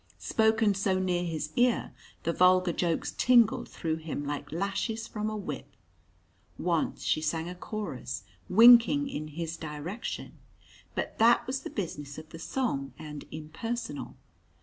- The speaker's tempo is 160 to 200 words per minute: No, average, 145 wpm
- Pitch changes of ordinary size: No, wide, 5.9 semitones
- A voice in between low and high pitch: Yes, medium, 180 Hz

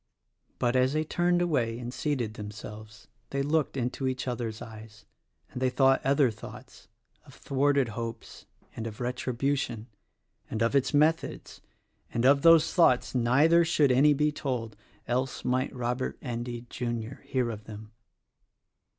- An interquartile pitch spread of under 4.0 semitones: Yes, average, 3.3 semitones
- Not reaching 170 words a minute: Yes, average, 155 wpm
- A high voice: No, low, 125 Hz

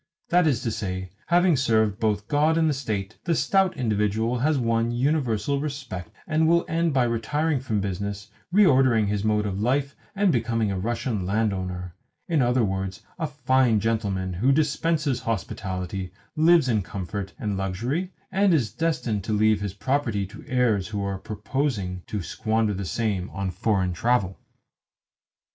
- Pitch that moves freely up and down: Yes, wide, 5.9 semitones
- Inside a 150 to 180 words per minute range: Yes, average, 160 wpm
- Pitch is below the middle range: Yes, low, 115 Hz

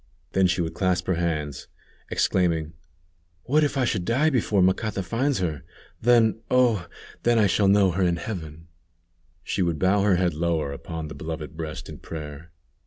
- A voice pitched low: Yes, very low, 90 Hz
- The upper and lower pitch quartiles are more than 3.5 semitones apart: Yes, average, 4.7 semitones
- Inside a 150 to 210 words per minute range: Yes, average, 175 wpm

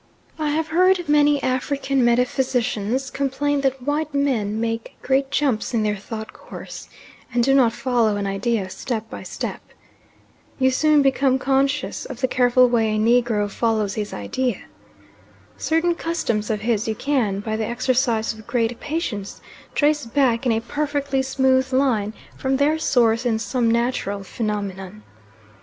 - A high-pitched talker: Yes, high, 245 Hz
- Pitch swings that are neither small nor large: Yes, average, 3.8 semitones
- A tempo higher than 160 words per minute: No, average, 150 wpm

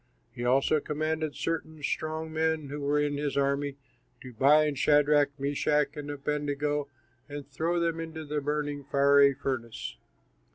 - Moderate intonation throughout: No, narrow, 1.6 semitones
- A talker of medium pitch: Yes, medium, 145 Hz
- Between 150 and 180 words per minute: No, average, 140 wpm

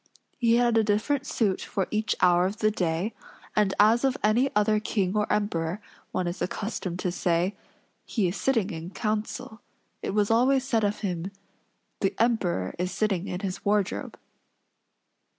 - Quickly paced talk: No, average, 165 wpm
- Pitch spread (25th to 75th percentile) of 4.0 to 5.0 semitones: No, average, 3.5 semitones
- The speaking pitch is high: Yes, high, 210 Hz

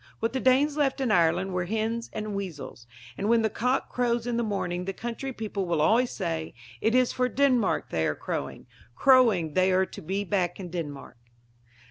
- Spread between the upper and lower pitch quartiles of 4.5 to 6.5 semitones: Yes, average, 5.3 semitones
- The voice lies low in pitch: No, high, 210 Hz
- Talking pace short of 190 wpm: No, average, 195 wpm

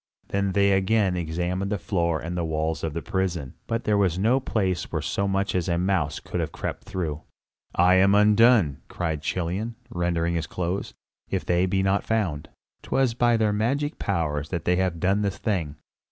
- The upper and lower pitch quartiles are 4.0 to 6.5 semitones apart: No, average, 3.3 semitones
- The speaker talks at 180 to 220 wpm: Yes, average, 190 wpm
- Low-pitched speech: Yes, very low, 95 Hz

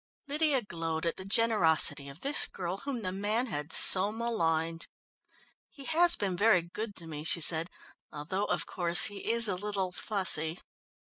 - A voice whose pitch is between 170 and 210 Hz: Yes, high, 190 Hz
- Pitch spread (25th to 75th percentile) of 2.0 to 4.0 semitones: No, wide, 5.4 semitones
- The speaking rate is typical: Yes, average, 165 wpm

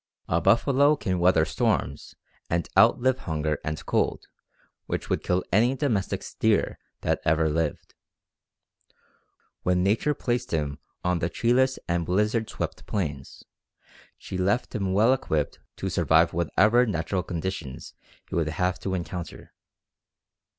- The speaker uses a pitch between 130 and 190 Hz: No, very low, 90 Hz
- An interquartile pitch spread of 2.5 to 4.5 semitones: No, wide, 5.5 semitones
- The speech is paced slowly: Yes, slow, 130 wpm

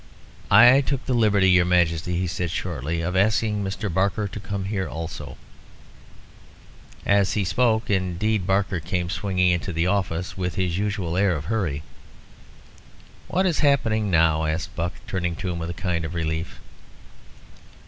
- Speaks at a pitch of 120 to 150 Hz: No, very low, 90 Hz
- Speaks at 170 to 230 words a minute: No, average, 160 wpm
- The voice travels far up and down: No, average, 3.2 semitones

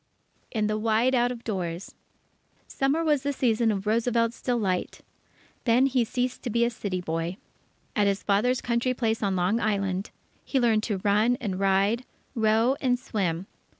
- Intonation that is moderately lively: Yes, average, 3.7 semitones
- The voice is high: Yes, high, 225 Hz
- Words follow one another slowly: No, average, 165 wpm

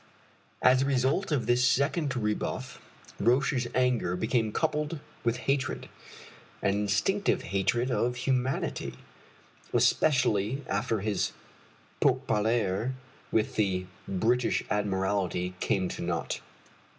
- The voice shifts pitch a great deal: No, average, 4.6 semitones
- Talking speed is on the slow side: Yes, slow, 100 wpm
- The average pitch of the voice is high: No, low, 120 Hz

